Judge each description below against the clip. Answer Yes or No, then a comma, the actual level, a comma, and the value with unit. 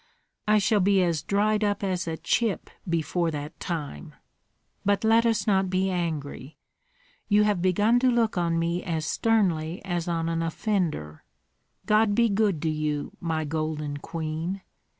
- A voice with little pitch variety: No, average, 4.4 semitones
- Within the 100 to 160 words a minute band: Yes, average, 155 wpm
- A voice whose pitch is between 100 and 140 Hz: No, medium, 175 Hz